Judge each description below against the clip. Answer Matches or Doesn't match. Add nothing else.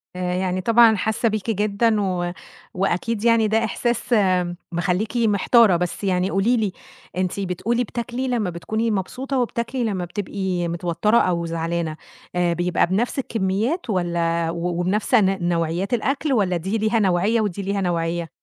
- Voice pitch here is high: Matches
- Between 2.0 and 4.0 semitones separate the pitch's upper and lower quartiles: Doesn't match